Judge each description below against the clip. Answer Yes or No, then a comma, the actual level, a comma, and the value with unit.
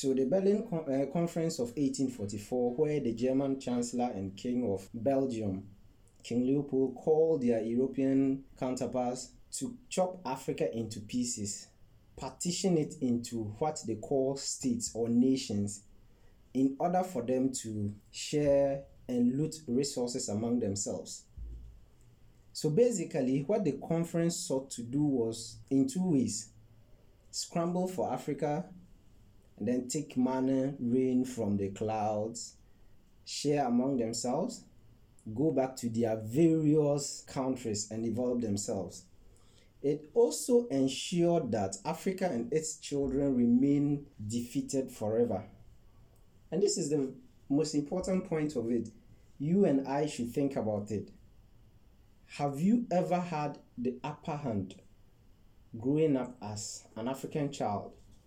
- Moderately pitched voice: No, low, 130 Hz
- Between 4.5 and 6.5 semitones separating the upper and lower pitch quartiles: Yes, average, 4.9 semitones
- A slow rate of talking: Yes, slow, 125 wpm